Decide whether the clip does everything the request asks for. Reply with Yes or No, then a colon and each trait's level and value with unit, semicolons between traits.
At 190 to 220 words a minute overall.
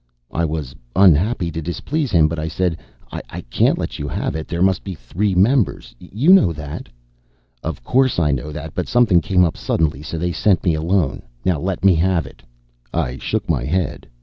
Yes: average, 200 wpm